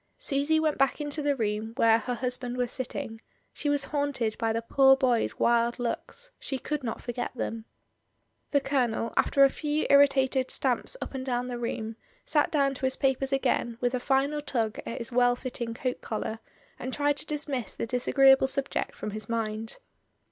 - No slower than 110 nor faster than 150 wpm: No, average, 185 wpm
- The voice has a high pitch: Yes, very high, 255 Hz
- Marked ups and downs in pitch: No, average, 3.1 semitones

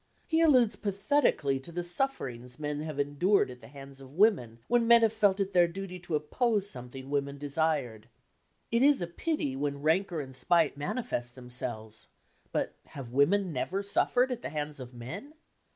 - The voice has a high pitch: No, medium, 155 Hz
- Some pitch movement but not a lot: No, wide, 7.0 semitones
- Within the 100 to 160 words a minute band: No, average, 175 wpm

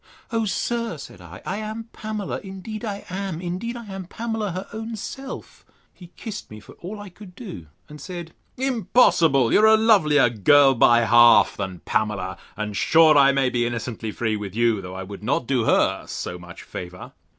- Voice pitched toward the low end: No, medium, 165 Hz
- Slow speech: No, average, 190 wpm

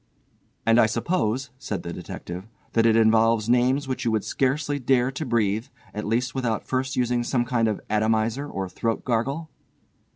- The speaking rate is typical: Yes, average, 170 wpm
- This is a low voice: Yes, low, 120 Hz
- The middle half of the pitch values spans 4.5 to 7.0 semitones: No, average, 3.0 semitones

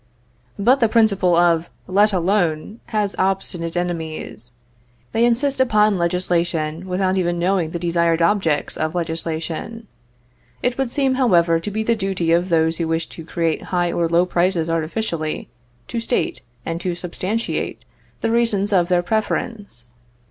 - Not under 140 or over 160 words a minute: Yes, average, 150 wpm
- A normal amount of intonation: Yes, average, 4.0 semitones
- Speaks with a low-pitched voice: No, medium, 180 Hz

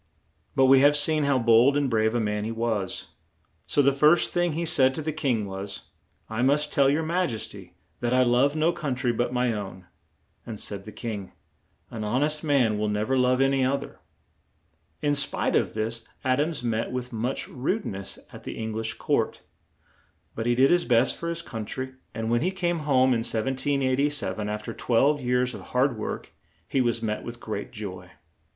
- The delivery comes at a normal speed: No, fast, 210 wpm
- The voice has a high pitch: No, low, 125 Hz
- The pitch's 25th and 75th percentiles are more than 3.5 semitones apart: Yes, average, 4.1 semitones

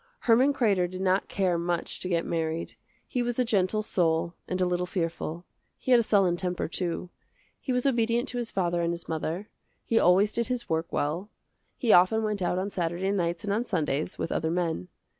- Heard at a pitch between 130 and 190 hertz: Yes, medium, 185 Hz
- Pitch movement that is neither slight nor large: Yes, average, 4.4 semitones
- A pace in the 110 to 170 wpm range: No, fast, 205 wpm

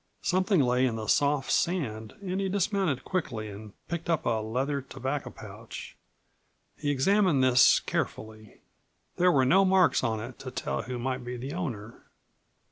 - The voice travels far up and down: Yes, wide, 7.1 semitones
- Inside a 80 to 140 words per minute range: No, average, 160 wpm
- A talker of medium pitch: No, low, 130 Hz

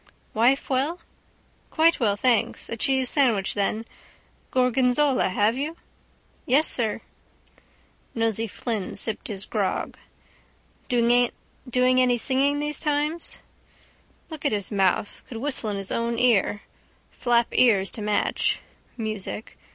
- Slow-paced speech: Yes, slow, 120 wpm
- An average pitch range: Yes, average, 3.7 semitones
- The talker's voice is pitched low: No, high, 240 Hz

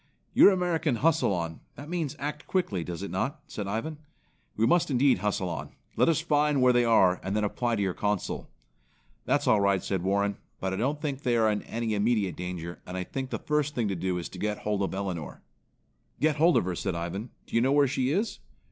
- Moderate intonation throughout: No, wide, 7.1 semitones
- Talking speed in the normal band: No, fast, 230 wpm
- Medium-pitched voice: No, low, 110 Hz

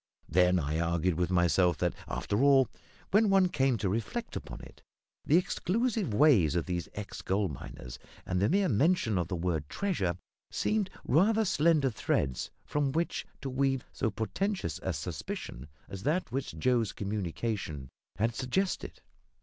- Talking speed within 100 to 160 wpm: Yes, average, 155 wpm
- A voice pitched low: Yes, low, 110 Hz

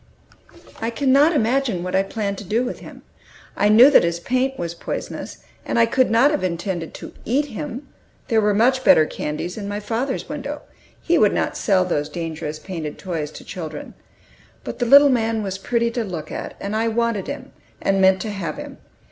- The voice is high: Yes, high, 215 Hz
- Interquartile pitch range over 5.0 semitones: Yes, wide, 5.6 semitones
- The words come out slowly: No, average, 200 wpm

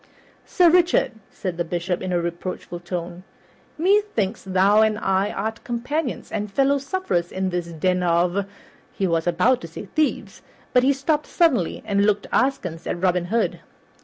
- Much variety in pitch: Yes, wide, 6.7 semitones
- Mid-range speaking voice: No, high, 195 Hz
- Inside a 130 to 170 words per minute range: Yes, average, 165 wpm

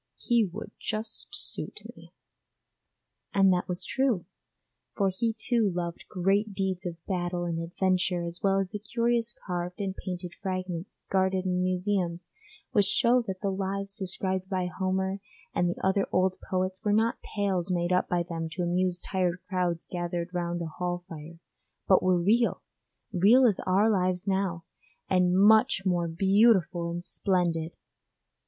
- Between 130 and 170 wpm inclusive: Yes, average, 155 wpm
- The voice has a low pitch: No, medium, 185 Hz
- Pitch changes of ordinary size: No, narrow, 2.1 semitones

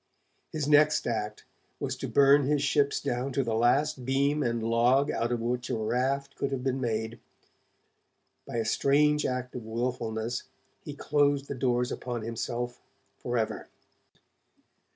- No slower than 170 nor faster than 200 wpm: No, average, 150 wpm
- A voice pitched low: Yes, low, 125 Hz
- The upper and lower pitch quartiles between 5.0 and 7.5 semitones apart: No, average, 3.0 semitones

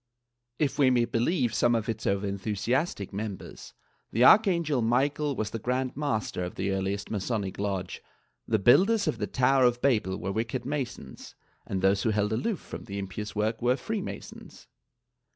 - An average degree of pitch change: Yes, average, 4.7 semitones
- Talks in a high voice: No, low, 115 Hz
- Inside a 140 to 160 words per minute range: No, average, 175 wpm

